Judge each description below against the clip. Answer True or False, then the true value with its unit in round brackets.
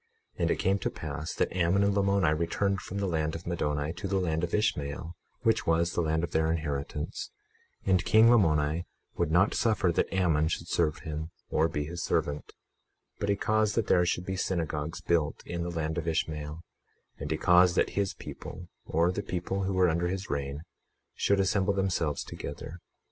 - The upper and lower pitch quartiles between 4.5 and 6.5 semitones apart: False (3.4 semitones)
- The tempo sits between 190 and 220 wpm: True (200 wpm)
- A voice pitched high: False (85 Hz)